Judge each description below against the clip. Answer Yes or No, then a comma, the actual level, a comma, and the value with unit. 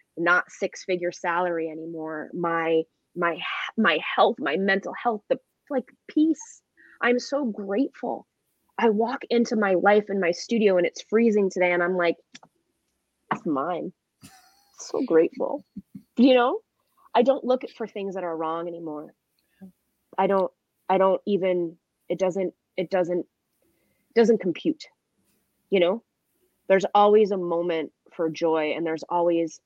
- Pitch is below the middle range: No, high, 190 Hz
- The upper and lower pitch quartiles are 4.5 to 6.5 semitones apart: Yes, wide, 5.5 semitones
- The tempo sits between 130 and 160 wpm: Yes, average, 140 wpm